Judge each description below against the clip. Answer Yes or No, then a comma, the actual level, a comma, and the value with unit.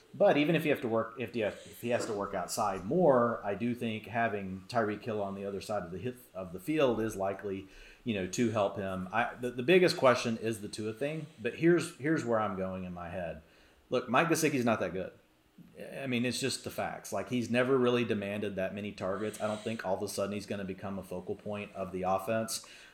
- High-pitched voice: No, low, 110 Hz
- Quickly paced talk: Yes, fast, 235 wpm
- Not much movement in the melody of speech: No, average, 4.0 semitones